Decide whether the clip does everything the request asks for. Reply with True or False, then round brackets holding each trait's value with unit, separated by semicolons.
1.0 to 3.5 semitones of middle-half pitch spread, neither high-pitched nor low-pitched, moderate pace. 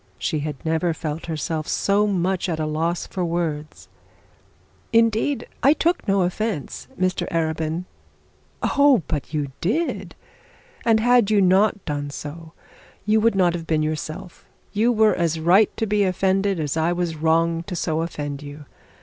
False (4.4 semitones; 175 Hz; 160 wpm)